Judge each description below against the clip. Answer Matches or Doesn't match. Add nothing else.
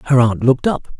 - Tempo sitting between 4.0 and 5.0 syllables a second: Doesn't match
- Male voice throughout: Matches